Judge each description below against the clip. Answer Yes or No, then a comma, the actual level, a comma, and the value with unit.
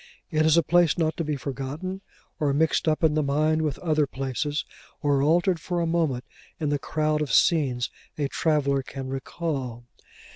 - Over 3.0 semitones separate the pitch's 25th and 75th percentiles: No, narrow, 2.6 semitones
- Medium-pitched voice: Yes, medium, 150 Hz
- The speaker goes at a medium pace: Yes, average, 180 wpm